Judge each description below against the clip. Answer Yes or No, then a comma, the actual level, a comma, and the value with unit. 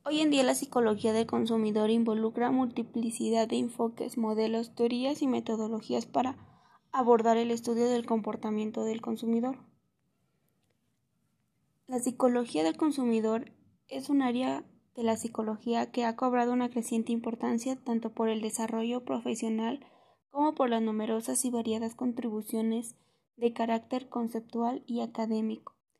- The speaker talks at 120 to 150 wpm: Yes, average, 130 wpm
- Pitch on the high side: Yes, high, 235 Hz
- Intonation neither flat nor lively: No, narrow, 1.7 semitones